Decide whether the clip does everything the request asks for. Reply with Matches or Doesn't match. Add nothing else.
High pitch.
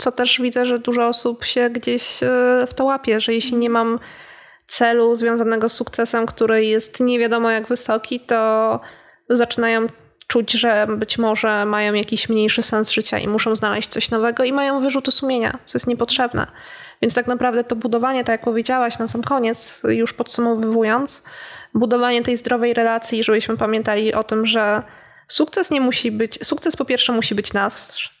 Matches